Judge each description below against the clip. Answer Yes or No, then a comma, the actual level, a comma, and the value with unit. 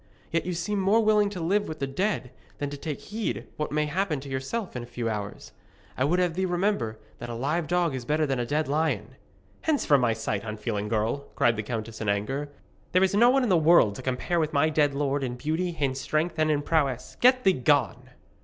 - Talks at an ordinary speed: No, fast, 235 wpm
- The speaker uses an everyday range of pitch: No, wide, 6.0 semitones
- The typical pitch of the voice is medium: Yes, medium, 145 Hz